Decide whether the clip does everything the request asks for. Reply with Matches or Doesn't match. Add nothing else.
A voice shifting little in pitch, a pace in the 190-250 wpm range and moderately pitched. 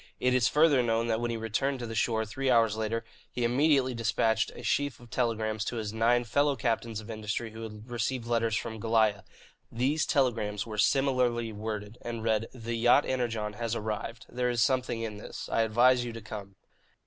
Doesn't match